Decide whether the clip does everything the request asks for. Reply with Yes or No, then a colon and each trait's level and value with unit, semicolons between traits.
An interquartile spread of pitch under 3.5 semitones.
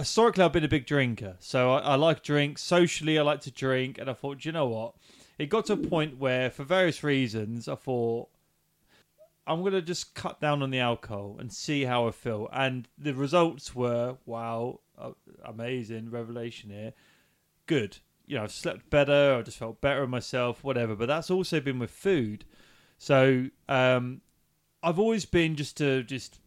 No: average, 4.2 semitones